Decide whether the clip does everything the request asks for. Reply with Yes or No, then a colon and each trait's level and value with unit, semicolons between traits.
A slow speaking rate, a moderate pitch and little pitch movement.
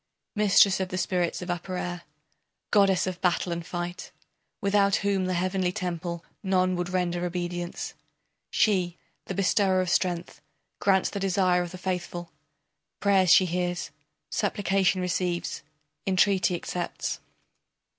Yes: slow, 130 wpm; medium, 180 Hz; narrow, 1.5 semitones